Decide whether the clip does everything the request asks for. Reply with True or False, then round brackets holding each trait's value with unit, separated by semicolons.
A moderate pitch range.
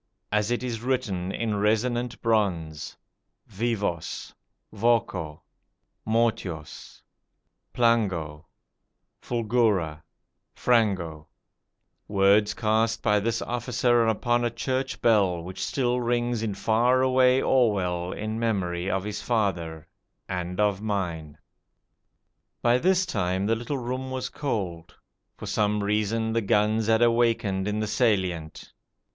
True (4.0 semitones)